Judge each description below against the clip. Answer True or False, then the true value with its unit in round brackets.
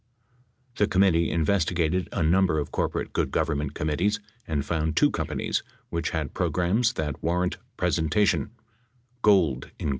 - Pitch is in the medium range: False (85 Hz)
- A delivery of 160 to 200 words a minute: False (140 wpm)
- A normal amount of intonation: True (3.4 semitones)